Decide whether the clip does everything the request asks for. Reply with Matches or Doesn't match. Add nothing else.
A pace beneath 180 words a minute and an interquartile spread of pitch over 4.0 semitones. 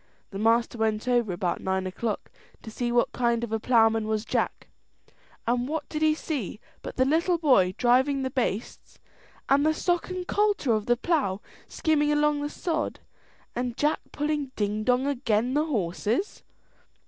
Matches